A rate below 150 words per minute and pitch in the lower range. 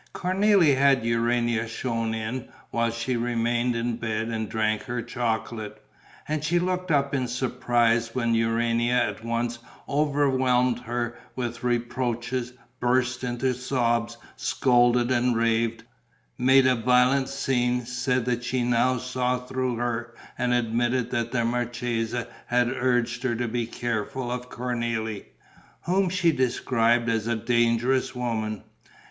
Yes: slow, 135 wpm; low, 120 Hz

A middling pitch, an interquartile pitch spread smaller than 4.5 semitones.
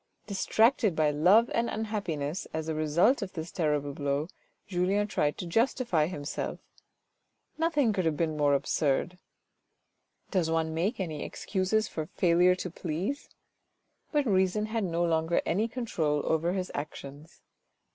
No: medium, 175 Hz; average, 5.0 semitones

